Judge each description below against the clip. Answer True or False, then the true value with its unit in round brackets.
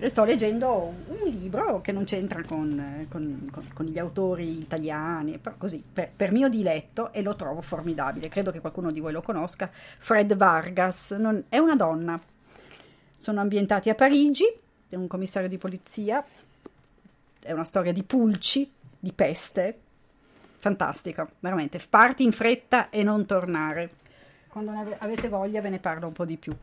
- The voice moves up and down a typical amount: True (4.8 semitones)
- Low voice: False (190 Hz)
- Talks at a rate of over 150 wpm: True (160 wpm)